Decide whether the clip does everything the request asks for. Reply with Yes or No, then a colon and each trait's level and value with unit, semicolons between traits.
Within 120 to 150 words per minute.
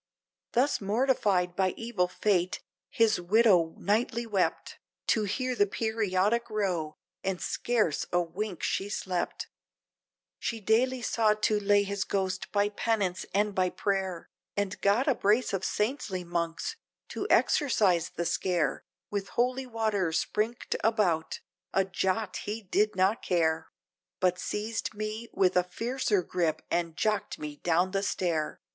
Yes: average, 140 wpm